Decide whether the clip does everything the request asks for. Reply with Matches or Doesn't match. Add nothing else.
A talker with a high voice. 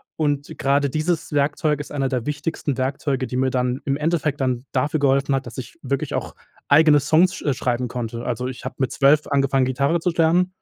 Doesn't match